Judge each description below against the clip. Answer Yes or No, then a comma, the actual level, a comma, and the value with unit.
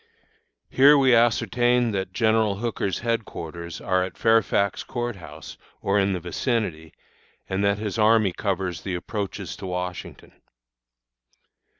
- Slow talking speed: Yes, slow, 125 wpm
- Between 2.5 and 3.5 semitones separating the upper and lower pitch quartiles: No, average, 3.9 semitones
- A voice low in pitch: Yes, low, 100 Hz